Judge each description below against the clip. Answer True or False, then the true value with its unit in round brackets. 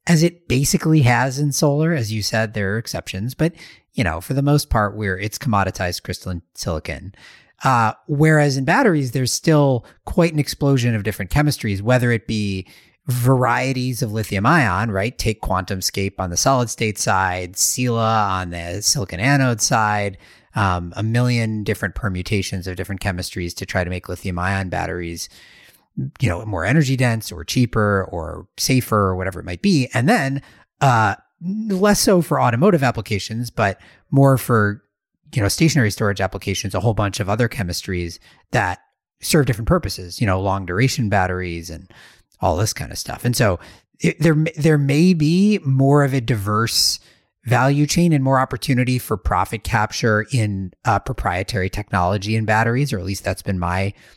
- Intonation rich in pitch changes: True (5.7 semitones)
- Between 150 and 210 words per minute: True (170 wpm)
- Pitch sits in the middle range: False (110 Hz)